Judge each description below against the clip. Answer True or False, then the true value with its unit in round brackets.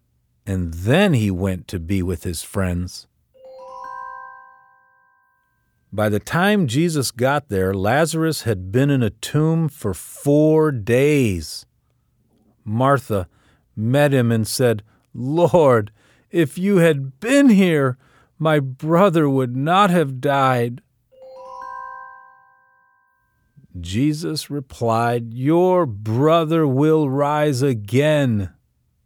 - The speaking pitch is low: True (125 Hz)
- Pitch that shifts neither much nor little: False (8.6 semitones)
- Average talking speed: False (100 wpm)